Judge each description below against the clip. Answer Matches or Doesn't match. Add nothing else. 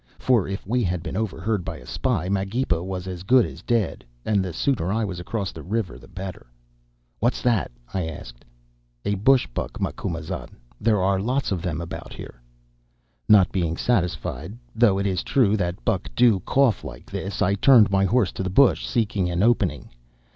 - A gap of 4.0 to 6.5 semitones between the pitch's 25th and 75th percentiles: Matches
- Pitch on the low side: Matches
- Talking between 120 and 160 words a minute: Doesn't match